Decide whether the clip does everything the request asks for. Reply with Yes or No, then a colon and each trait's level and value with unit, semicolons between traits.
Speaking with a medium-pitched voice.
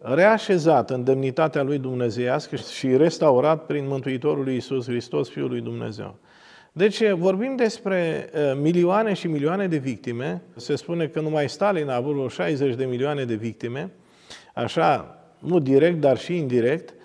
Yes: medium, 145 Hz